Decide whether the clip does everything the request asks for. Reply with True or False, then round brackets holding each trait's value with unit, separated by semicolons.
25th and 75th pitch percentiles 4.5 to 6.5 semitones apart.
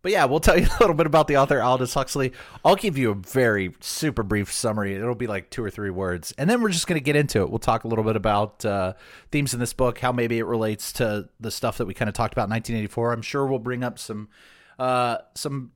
False (3.7 semitones)